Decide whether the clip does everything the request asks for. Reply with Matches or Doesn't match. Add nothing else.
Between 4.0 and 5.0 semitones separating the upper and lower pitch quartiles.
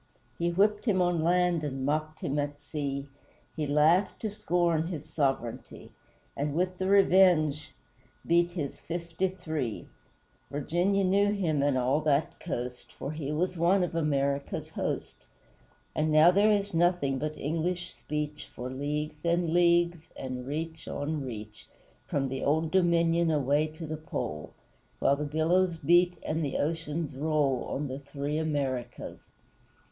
Doesn't match